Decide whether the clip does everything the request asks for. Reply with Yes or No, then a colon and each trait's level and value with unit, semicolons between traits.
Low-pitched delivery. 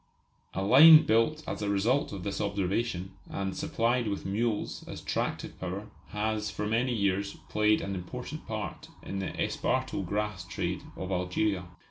Yes: low, 105 Hz